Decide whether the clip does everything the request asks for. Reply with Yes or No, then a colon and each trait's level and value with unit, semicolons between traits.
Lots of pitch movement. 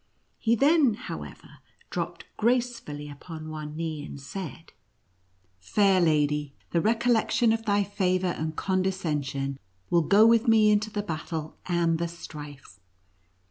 Yes: wide, 6.1 semitones